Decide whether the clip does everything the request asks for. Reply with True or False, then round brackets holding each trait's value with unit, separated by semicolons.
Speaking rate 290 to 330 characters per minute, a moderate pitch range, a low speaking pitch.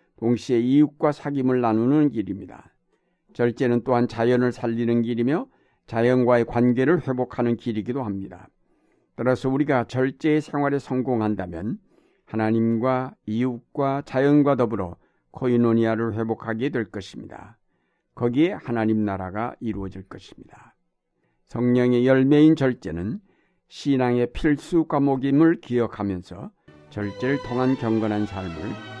True (295 characters per minute; 3.2 semitones; 120 Hz)